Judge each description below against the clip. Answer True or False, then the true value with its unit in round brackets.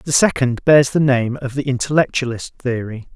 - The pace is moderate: True (170 wpm)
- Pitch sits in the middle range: False (130 Hz)